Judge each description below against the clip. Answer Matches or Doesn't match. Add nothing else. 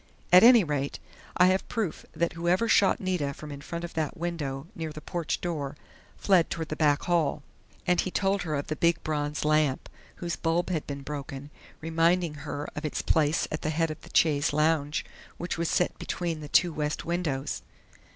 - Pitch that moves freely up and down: Doesn't match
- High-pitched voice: Doesn't match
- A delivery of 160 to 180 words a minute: Doesn't match